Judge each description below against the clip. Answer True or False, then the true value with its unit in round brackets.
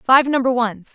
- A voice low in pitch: False (250 Hz)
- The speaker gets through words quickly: False (190 wpm)